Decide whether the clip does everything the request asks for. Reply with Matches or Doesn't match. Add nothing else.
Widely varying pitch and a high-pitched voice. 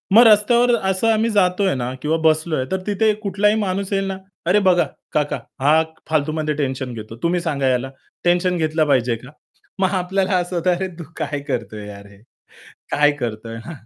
Doesn't match